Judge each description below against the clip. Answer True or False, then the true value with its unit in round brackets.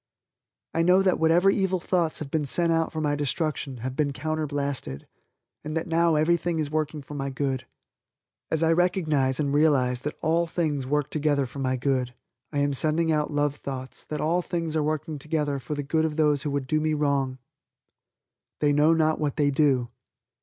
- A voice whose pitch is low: False (150 Hz)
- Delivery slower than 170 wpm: False (195 wpm)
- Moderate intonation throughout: False (2.3 semitones)